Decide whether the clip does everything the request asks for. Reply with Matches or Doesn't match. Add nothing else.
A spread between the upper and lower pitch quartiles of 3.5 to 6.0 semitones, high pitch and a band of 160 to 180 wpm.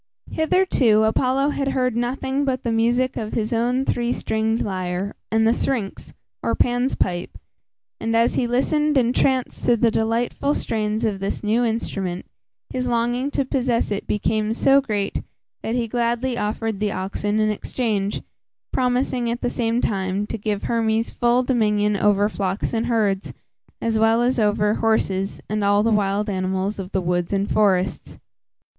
Doesn't match